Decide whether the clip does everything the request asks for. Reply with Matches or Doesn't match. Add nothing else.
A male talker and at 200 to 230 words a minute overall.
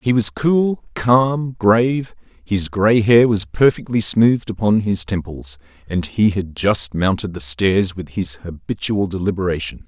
Doesn't match